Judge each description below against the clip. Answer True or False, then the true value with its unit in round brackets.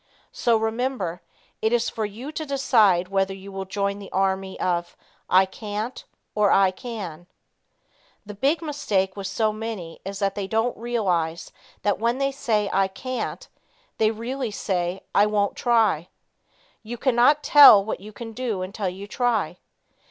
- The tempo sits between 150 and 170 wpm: True (160 wpm)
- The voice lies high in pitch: True (210 Hz)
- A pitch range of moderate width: True (3.7 semitones)